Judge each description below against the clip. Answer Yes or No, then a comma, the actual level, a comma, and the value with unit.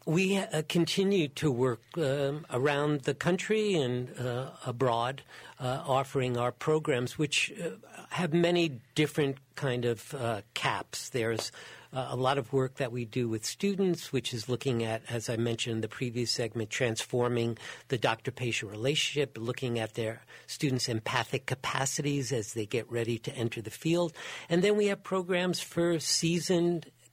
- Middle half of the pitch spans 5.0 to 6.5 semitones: Yes, average, 5.3 semitones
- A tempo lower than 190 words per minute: Yes, average, 160 wpm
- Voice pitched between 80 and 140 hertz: Yes, low, 135 Hz